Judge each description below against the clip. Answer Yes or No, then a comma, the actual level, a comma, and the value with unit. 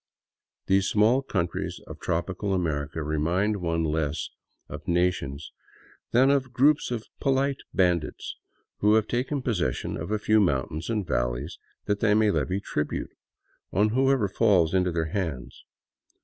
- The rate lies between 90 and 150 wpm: Yes, average, 145 wpm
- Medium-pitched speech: No, very low, 95 Hz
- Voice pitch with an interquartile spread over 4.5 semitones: Yes, average, 5.1 semitones